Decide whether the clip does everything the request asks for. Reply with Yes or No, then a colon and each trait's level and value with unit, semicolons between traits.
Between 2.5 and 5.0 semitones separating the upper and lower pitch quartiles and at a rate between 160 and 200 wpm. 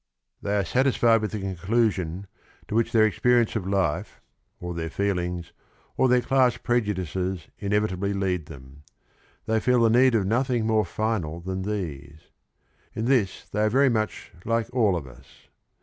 Yes: average, 4.3 semitones; average, 165 wpm